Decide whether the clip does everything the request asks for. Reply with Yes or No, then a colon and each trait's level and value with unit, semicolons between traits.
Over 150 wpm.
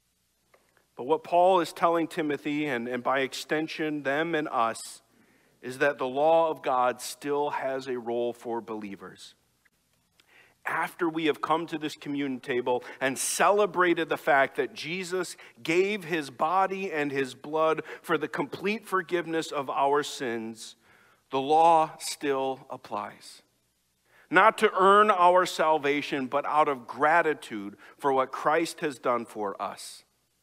No: average, 140 wpm